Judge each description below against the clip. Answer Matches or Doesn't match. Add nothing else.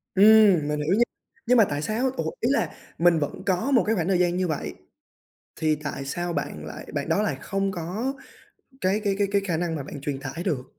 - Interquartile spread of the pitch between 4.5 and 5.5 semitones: Matches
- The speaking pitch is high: Doesn't match